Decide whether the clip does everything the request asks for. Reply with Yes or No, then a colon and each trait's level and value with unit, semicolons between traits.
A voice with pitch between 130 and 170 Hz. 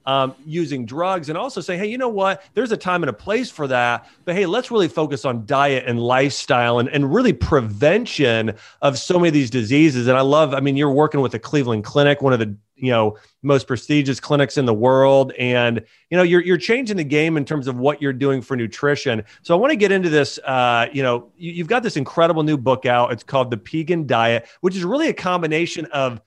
Yes: medium, 140 Hz